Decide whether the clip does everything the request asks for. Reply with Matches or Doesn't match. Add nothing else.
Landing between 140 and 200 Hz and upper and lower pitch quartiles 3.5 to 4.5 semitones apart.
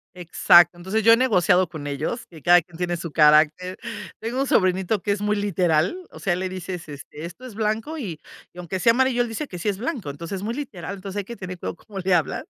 Matches